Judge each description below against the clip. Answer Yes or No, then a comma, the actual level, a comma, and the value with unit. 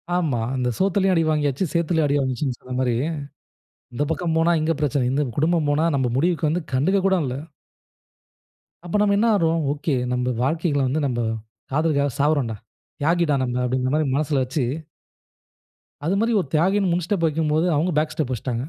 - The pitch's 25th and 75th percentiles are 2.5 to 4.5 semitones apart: Yes, average, 4.1 semitones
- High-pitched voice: No, medium, 155 Hz